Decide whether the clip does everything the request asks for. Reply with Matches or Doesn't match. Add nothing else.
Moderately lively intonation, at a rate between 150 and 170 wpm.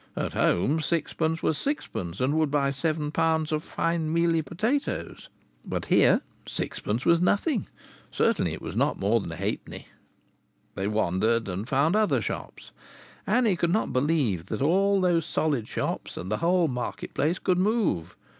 Doesn't match